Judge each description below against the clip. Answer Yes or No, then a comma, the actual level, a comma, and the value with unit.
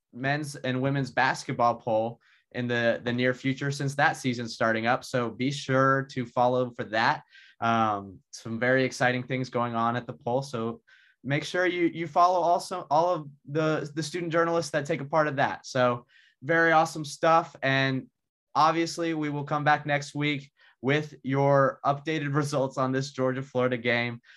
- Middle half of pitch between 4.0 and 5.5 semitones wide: No, average, 3.5 semitones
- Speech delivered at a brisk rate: No, average, 175 wpm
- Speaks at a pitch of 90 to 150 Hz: Yes, low, 135 Hz